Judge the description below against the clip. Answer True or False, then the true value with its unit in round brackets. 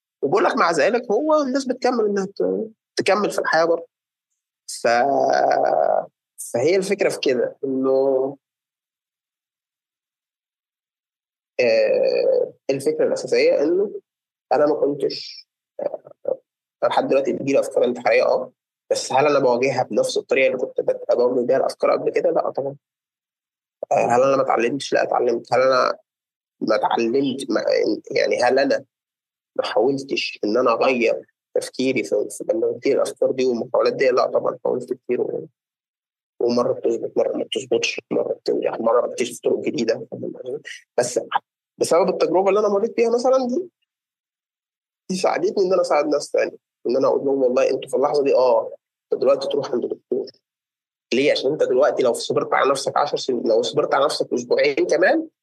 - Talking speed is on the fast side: True (145 wpm)